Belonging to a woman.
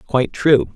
No: male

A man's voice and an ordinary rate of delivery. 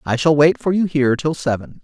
No: male; fast, 260 wpm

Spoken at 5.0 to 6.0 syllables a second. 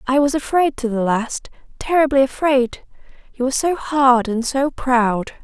No: 4.5 syllables/s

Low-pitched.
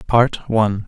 Yes: low, 110 Hz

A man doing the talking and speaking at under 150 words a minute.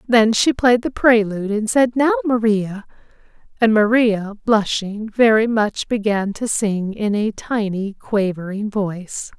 No: female; average, 140 wpm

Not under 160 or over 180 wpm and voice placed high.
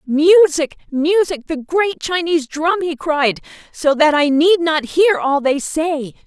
Yes: average, 165 wpm; very high, 315 Hz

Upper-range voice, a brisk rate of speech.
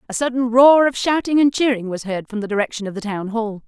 Yes: high, 230 Hz; fast, 260 wpm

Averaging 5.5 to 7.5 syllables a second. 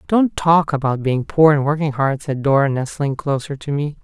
No: 4.9 syllables/s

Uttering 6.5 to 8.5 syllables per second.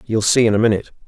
Yes: 8.1 syllables/s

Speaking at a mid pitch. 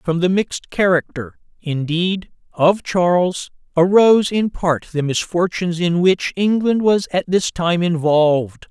Yes: medium, 175 Hz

